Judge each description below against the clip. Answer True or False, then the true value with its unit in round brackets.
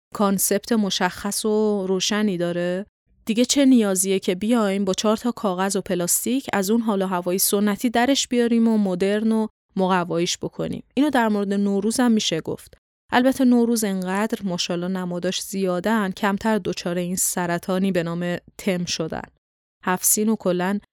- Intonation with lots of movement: False (3.2 semitones)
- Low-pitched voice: False (200 Hz)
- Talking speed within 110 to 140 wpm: False (150 wpm)